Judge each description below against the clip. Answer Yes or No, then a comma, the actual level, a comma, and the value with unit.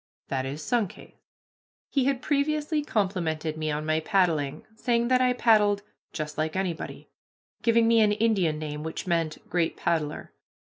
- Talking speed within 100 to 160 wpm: Yes, average, 150 wpm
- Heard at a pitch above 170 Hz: Yes, medium, 185 Hz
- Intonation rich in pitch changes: Yes, wide, 6.9 semitones